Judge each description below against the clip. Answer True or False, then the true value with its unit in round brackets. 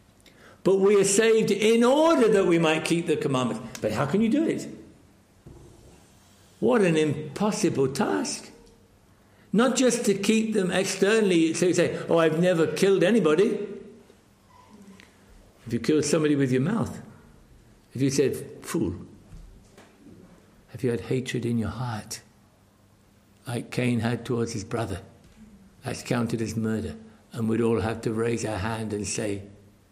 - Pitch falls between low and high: False (130 Hz)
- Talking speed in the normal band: True (150 wpm)